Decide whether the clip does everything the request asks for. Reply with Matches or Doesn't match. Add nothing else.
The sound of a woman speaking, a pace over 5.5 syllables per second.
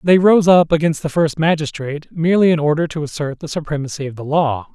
Doesn't match